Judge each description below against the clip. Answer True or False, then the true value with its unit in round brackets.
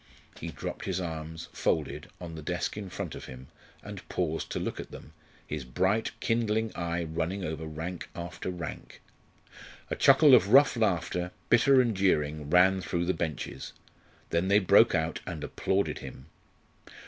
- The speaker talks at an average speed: True (160 wpm)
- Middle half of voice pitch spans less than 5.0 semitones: True (3.7 semitones)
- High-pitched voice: False (90 Hz)